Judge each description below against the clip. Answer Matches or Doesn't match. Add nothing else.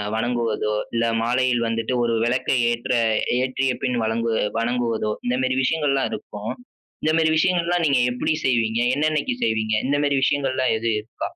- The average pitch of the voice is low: Matches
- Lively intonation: Doesn't match